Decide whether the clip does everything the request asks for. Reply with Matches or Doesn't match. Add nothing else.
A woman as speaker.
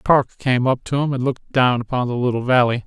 Doesn't match